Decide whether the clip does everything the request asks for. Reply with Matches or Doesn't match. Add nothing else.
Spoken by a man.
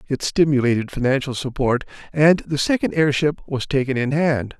Matches